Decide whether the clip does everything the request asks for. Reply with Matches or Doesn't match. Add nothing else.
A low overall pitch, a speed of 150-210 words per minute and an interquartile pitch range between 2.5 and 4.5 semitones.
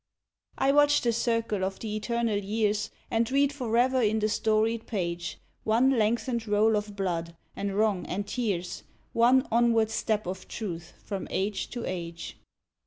Doesn't match